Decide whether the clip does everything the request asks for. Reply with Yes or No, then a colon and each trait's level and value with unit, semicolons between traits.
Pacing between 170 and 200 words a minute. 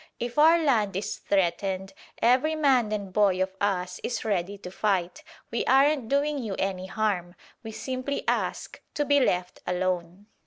No: average, 160 wpm